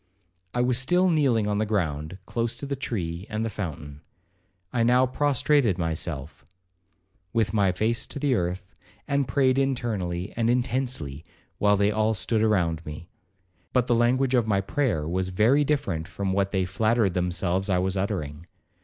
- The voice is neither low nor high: No, low, 105 Hz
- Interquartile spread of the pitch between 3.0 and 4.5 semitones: No, wide, 5.5 semitones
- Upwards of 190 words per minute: No, average, 165 wpm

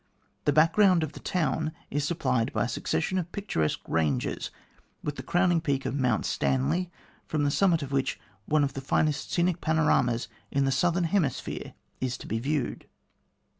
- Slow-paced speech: No, average, 170 wpm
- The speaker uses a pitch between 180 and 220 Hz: No, medium, 145 Hz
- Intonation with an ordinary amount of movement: Yes, average, 4.3 semitones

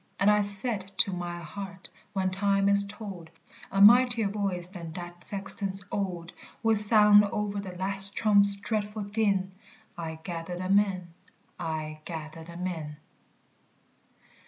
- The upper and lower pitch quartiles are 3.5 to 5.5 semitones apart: No, narrow, 2.6 semitones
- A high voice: Yes, high, 195 Hz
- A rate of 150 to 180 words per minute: No, slow, 135 wpm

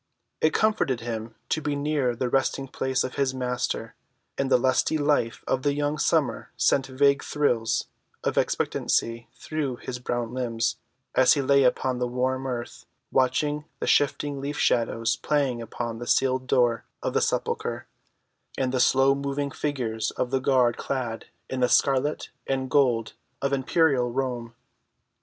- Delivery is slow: No, average, 150 wpm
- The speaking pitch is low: Yes, low, 130 Hz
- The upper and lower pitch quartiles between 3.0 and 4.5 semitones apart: No, narrow, 2.4 semitones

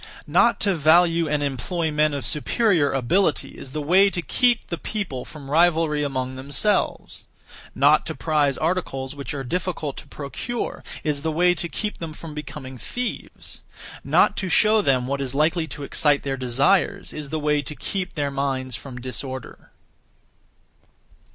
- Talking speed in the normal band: Yes, average, 165 wpm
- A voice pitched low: No, medium, 150 Hz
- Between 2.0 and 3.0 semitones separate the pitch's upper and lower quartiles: No, average, 4.2 semitones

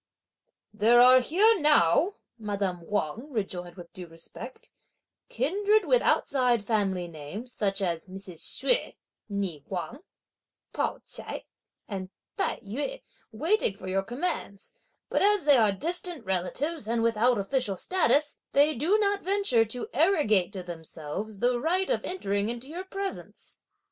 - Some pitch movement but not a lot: No, wide, 8.8 semitones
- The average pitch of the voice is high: Yes, high, 230 Hz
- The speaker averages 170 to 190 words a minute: No, average, 140 wpm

